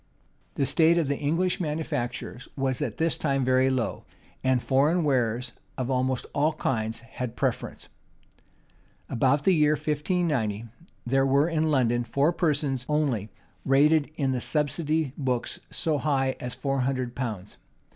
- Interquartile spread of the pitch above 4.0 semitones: No, average, 3.3 semitones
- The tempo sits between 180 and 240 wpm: No, average, 145 wpm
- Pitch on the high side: No, low, 135 Hz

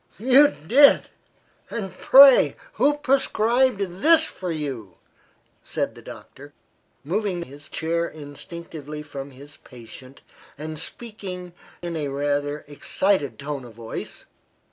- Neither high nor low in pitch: Yes, medium, 165 Hz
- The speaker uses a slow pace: Yes, slow, 115 wpm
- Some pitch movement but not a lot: No, wide, 6.7 semitones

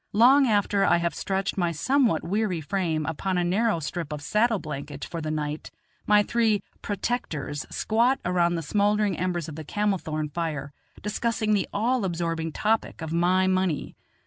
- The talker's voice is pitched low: No, medium, 185 Hz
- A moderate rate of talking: Yes, average, 170 wpm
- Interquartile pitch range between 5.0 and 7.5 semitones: No, average, 4.6 semitones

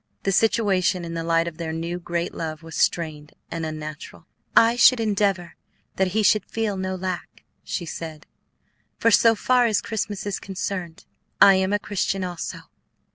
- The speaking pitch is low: No, medium, 185 Hz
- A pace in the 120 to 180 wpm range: Yes, average, 170 wpm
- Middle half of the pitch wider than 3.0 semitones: Yes, average, 3.6 semitones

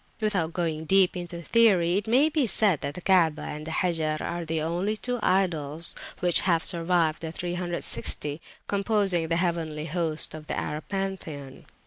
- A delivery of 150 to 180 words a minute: Yes, average, 165 wpm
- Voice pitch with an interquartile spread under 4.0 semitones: Yes, average, 3.3 semitones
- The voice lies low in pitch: No, medium, 170 Hz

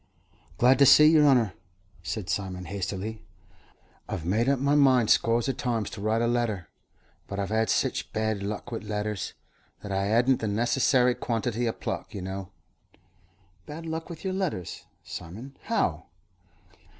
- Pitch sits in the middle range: No, low, 110 Hz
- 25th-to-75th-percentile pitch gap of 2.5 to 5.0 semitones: Yes, average, 4.4 semitones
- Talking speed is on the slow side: No, average, 160 wpm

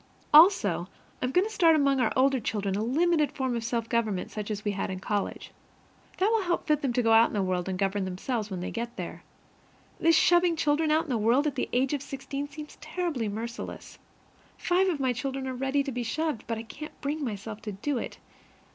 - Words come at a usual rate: No, fast, 225 wpm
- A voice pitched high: Yes, very high, 255 Hz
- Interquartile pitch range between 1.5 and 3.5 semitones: No, wide, 5.6 semitones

